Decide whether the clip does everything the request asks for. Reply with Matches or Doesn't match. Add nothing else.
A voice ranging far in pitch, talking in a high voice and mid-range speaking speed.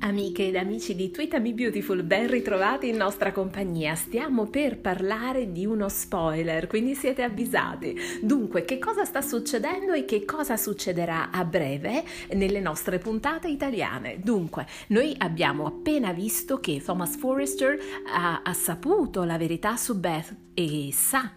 Matches